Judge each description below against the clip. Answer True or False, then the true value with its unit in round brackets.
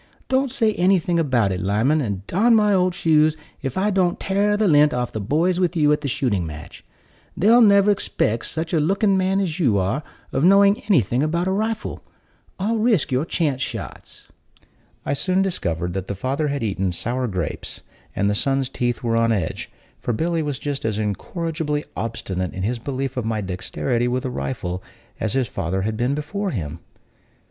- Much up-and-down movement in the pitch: True (8.8 semitones)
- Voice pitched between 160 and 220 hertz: False (140 Hz)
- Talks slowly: False (190 wpm)